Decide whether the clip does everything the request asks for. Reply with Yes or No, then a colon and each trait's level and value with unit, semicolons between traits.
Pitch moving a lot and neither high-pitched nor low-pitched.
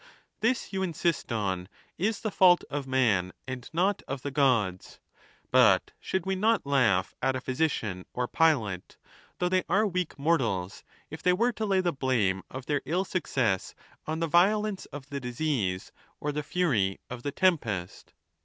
Yes: wide, 7.5 semitones; medium, 145 Hz